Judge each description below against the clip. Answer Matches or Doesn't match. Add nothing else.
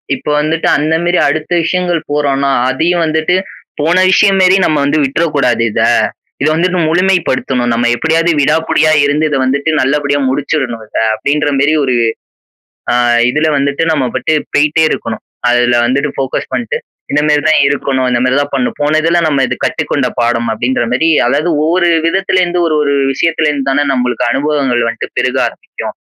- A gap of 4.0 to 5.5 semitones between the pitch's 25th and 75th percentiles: Doesn't match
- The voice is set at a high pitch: Doesn't match